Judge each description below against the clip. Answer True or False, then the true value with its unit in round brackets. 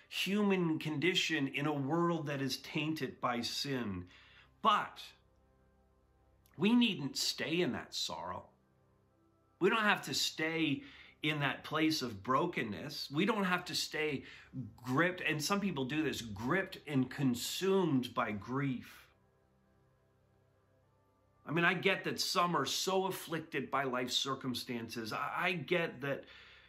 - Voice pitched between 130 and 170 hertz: True (135 Hz)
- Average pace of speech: False (130 wpm)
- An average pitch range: False (6.0 semitones)